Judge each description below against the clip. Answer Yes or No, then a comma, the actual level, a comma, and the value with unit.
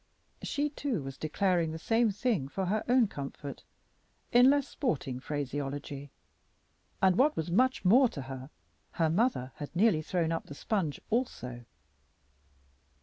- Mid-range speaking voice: Yes, medium, 170 Hz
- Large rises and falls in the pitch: Yes, wide, 8.6 semitones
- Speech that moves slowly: No, average, 145 wpm